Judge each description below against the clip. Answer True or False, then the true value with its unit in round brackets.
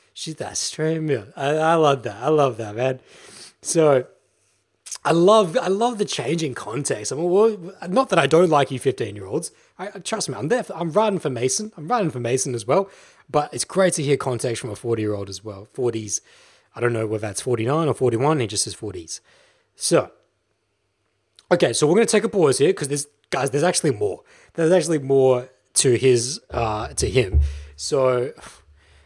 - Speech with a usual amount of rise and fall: False (6.8 semitones)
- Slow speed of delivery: False (190 wpm)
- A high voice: False (135 Hz)